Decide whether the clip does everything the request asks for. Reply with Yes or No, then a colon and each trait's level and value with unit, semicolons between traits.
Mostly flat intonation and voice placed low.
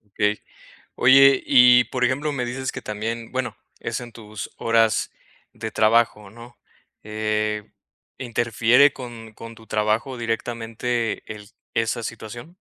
Yes: narrow, 2.2 semitones; low, 115 Hz